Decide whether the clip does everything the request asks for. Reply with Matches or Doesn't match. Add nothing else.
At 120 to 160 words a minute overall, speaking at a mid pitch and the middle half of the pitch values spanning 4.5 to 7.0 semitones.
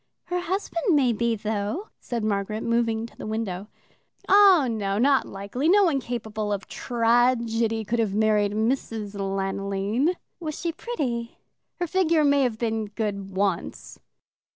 Doesn't match